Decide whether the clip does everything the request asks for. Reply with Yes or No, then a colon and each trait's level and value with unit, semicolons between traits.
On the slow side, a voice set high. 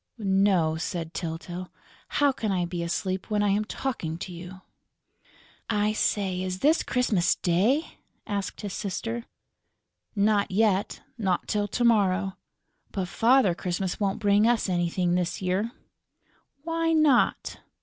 Yes: slow, 130 wpm; high, 195 Hz